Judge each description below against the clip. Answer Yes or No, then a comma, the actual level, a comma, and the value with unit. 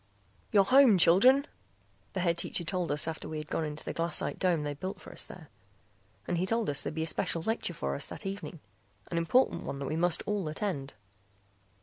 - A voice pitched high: No, medium, 170 Hz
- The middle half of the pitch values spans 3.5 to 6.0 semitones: Yes, average, 4.0 semitones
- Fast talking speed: Yes, fast, 215 wpm